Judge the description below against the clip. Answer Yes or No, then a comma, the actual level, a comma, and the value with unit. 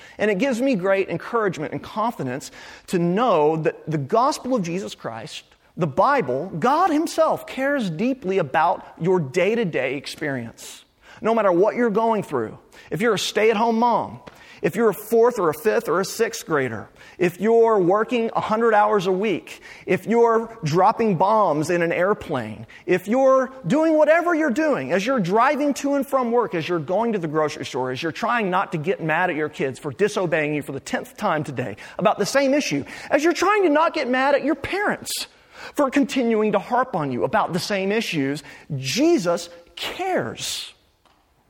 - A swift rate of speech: No, average, 190 wpm